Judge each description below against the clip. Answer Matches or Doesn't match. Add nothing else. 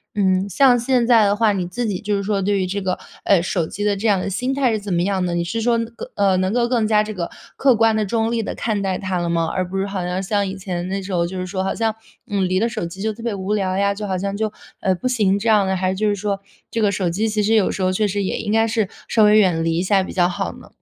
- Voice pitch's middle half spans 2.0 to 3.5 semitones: Matches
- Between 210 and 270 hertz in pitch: Doesn't match